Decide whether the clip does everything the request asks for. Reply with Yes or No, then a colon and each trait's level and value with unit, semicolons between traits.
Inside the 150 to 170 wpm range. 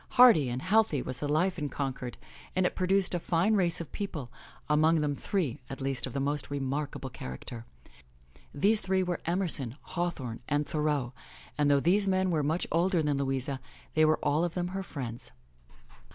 No: average, 180 wpm